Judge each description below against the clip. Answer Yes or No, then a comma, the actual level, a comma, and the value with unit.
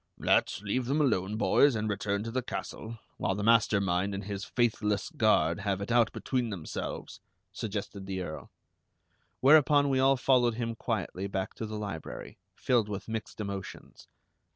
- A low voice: Yes, low, 105 Hz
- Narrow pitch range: No, average, 3.5 semitones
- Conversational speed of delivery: Yes, average, 165 wpm